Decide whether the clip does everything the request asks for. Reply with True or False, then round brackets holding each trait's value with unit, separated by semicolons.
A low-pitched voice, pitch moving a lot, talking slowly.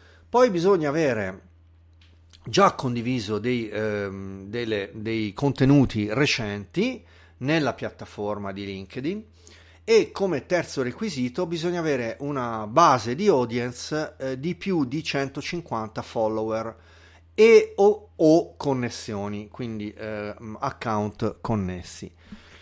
True (120 Hz; 6.2 semitones; 105 wpm)